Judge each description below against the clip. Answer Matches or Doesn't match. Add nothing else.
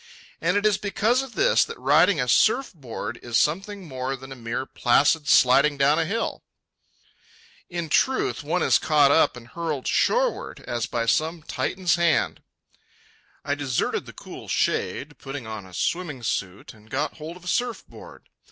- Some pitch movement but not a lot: Doesn't match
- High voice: Doesn't match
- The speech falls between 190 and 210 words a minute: Doesn't match